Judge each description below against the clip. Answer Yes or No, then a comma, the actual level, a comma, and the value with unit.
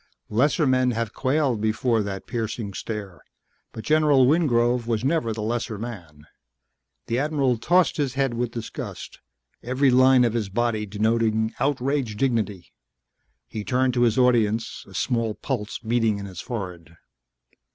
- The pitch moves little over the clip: No, average, 3.2 semitones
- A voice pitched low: Yes, low, 115 Hz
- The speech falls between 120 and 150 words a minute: Yes, average, 145 wpm